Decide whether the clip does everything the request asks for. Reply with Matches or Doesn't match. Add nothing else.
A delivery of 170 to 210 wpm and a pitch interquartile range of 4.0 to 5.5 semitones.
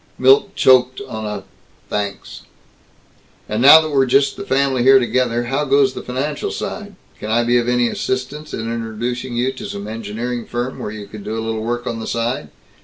Doesn't match